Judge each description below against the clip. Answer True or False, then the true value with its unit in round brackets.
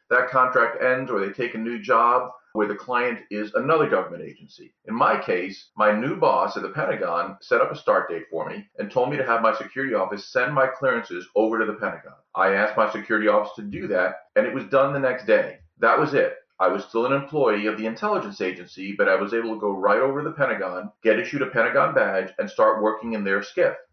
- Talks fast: True (240 wpm)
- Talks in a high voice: False (115 Hz)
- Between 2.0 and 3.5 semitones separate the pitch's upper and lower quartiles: False (4.7 semitones)